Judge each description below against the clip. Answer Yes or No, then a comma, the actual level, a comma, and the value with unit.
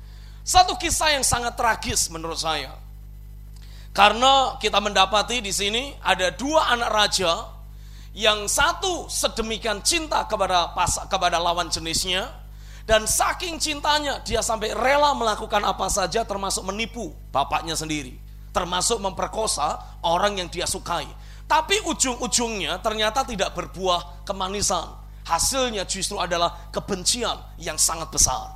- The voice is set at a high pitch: Yes, high, 195 Hz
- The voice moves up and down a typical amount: No, wide, 6.2 semitones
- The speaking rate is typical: Yes, average, 120 wpm